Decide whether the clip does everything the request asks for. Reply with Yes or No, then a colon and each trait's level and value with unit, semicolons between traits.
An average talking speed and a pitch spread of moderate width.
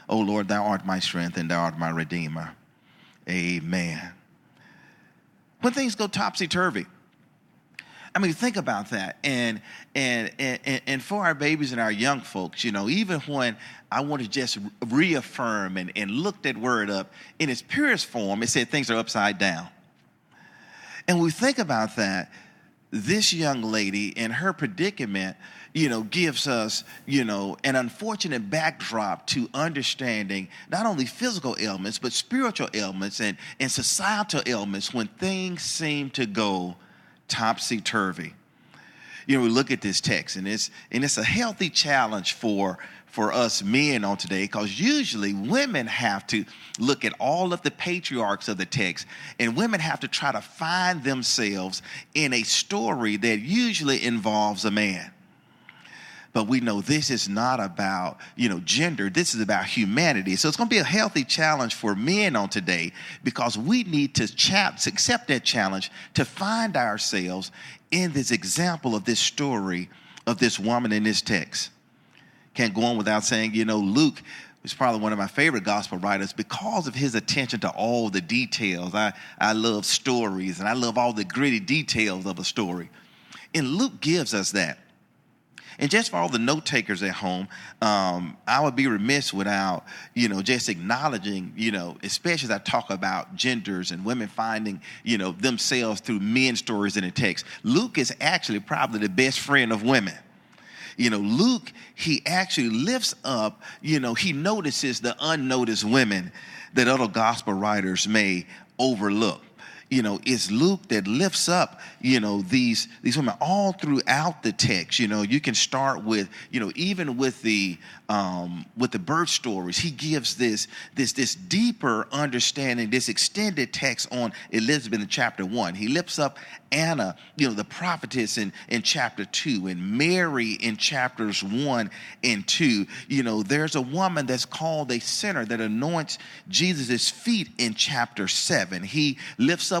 No: average, 170 wpm; wide, 6.7 semitones